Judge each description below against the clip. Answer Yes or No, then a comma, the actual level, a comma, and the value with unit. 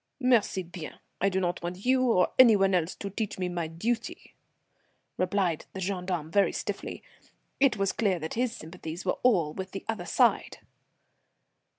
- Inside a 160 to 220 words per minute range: Yes, average, 170 wpm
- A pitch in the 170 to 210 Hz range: Yes, high, 190 Hz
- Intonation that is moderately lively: Yes, average, 4.0 semitones